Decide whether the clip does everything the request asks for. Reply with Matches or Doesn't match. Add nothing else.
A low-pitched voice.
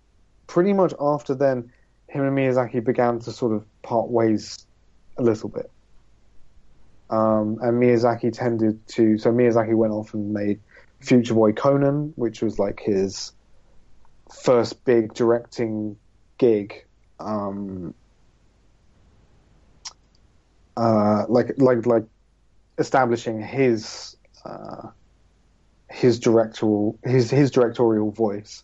Matches